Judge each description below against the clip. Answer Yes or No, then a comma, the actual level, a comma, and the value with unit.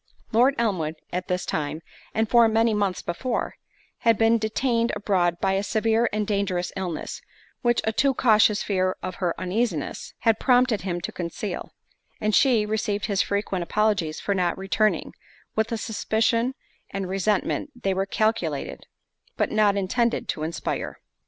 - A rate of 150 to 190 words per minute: Yes, average, 155 wpm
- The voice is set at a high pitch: Yes, high, 210 Hz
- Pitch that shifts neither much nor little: Yes, average, 3.5 semitones